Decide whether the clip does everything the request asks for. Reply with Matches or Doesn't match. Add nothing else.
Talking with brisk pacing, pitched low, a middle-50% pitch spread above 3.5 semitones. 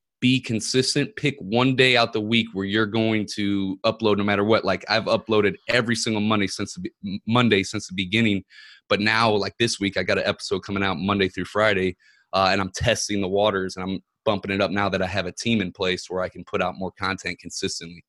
Doesn't match